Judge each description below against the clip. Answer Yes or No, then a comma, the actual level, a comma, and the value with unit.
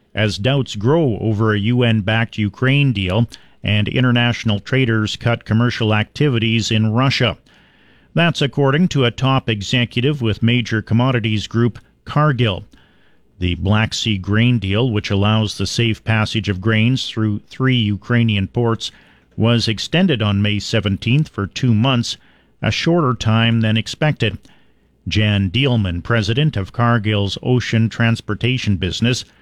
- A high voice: No, low, 115 Hz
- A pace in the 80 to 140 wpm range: Yes, slow, 135 wpm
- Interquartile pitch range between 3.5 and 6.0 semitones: No, average, 2.7 semitones